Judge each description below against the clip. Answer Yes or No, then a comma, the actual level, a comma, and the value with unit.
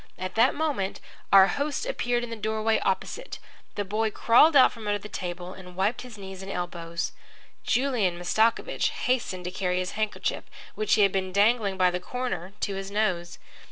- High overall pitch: Yes, high, 200 Hz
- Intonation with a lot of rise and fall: No, average, 3.7 semitones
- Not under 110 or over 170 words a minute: No, average, 185 wpm